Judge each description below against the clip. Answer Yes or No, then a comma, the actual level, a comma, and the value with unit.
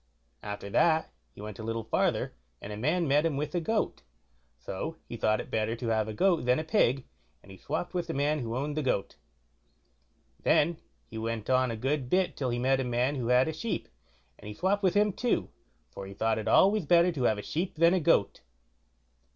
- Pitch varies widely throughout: Yes, wide, 6.7 semitones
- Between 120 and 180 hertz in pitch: Yes, low, 135 Hz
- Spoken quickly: Yes, fast, 225 wpm